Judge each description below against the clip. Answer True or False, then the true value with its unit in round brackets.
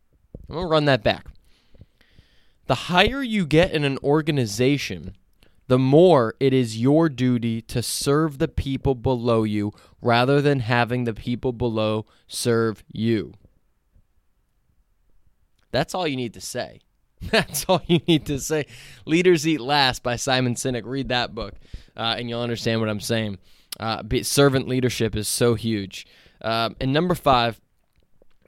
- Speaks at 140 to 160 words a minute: True (150 wpm)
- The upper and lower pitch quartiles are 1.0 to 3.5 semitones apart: False (4.2 semitones)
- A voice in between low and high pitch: False (125 Hz)